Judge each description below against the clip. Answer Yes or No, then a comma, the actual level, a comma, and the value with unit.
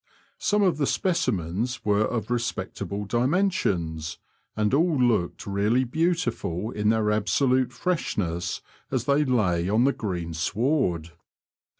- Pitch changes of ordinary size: No, wide, 6.0 semitones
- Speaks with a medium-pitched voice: No, low, 115 Hz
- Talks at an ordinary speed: No, slow, 120 wpm